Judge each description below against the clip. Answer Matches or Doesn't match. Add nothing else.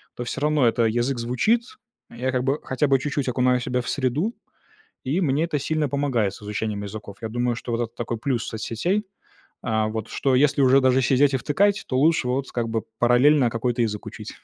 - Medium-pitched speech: Doesn't match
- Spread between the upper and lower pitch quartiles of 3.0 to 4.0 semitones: Matches